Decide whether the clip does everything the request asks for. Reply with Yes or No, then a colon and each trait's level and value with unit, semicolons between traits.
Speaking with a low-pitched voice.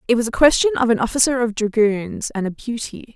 No: high, 235 Hz